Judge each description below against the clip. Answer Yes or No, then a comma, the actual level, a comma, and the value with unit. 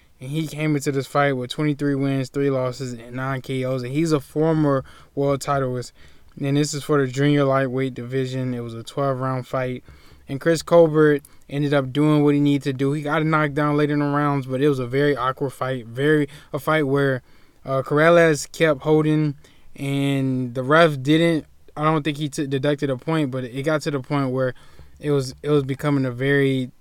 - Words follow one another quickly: Yes, fast, 210 wpm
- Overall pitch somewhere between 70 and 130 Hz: No, medium, 140 Hz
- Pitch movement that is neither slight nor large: No, narrow, 2.3 semitones